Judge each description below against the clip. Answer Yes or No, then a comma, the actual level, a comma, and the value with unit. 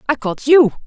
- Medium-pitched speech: No, very high, 260 Hz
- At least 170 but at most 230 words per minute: Yes, fast, 210 wpm